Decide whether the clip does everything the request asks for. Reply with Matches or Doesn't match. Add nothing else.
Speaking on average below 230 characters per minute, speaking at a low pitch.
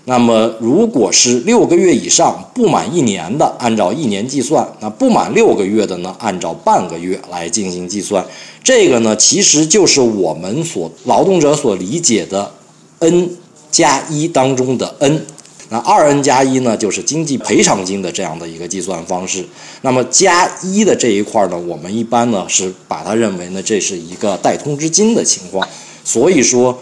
Doesn't match